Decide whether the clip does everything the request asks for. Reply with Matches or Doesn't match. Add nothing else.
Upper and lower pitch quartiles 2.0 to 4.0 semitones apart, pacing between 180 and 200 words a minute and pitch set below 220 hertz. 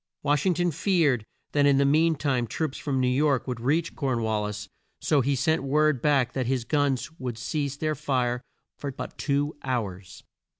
Matches